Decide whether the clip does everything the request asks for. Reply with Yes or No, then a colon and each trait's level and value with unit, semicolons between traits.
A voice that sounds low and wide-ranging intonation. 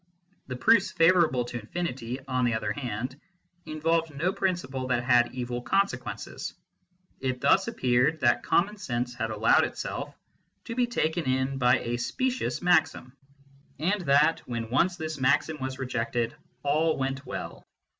No: low, 130 Hz; average, 5.0 semitones